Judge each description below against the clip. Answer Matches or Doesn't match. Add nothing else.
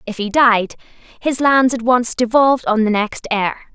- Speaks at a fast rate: Doesn't match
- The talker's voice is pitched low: Doesn't match